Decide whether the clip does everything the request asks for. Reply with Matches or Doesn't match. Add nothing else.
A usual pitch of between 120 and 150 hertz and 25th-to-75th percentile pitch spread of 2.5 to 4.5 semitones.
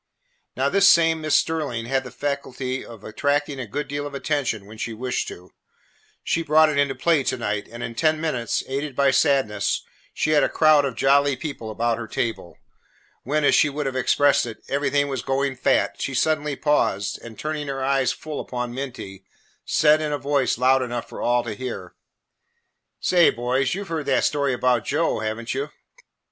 Matches